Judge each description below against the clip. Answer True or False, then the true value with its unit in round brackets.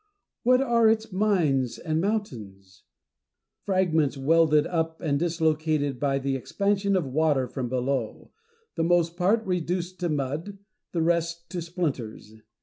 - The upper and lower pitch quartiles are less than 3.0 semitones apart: False (4.8 semitones)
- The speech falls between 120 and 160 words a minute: True (135 wpm)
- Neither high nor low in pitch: True (165 Hz)